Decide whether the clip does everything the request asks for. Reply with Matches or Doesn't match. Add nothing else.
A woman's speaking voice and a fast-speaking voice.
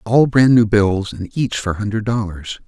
Doesn't match